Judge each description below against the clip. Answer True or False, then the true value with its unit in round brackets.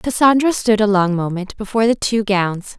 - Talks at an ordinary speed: True (195 wpm)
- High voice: True (210 Hz)